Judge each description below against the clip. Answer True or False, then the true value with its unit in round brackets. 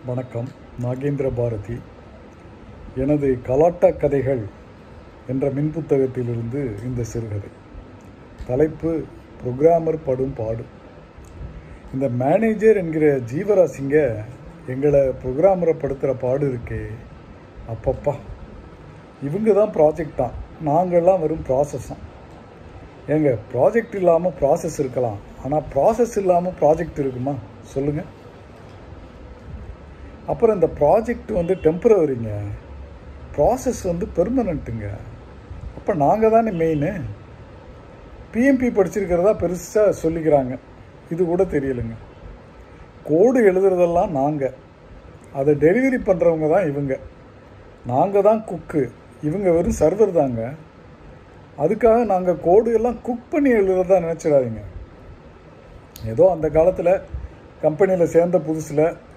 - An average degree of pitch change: False (6.9 semitones)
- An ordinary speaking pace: True (90 wpm)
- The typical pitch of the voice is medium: True (145 Hz)